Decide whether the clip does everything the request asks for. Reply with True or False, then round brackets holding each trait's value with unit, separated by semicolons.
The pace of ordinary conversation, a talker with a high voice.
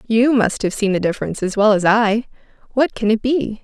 False (230 wpm; 220 Hz)